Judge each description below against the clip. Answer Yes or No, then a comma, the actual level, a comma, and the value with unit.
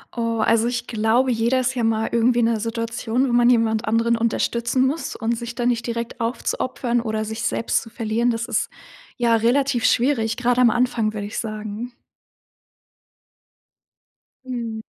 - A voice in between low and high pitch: No, high, 235 Hz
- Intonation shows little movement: Yes, narrow, 1.4 semitones